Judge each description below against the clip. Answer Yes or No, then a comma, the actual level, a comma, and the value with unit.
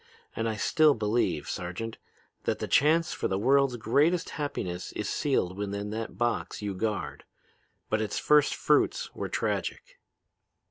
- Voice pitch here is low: Yes, low, 110 Hz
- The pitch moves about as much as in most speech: No, wide, 5.9 semitones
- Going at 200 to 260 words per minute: No, average, 145 wpm